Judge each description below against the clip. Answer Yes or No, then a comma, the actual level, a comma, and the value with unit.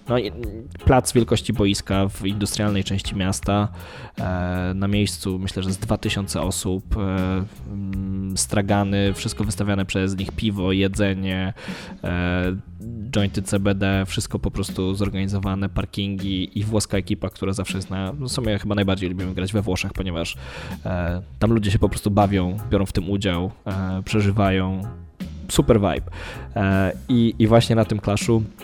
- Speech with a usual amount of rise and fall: No, narrow, 1.7 semitones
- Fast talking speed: No, average, 135 wpm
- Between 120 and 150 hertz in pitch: No, low, 100 Hz